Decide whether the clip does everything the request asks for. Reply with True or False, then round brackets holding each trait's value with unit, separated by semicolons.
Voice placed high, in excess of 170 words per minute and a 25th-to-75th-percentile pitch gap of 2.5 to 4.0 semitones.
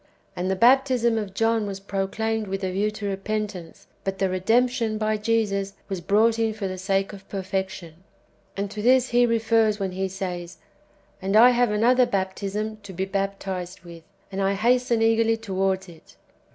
True (200 Hz; 180 wpm; 2.8 semitones)